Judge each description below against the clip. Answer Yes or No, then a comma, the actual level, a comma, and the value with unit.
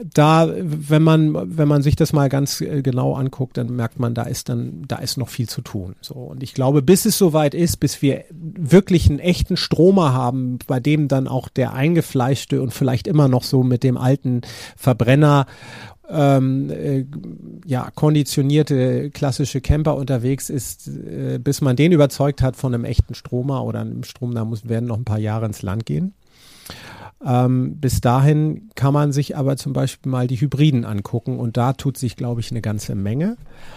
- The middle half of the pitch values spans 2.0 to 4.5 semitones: Yes, average, 3.2 semitones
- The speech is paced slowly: No, average, 185 wpm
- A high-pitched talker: No, low, 135 Hz